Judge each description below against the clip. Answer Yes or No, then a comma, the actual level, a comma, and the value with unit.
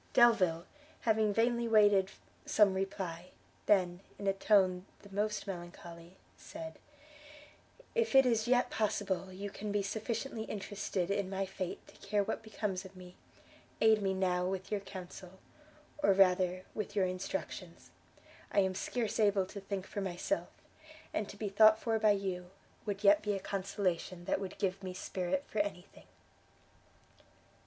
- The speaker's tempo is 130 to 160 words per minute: Yes, average, 155 wpm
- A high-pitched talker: Yes, high, 195 Hz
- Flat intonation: Yes, narrow, 2.3 semitones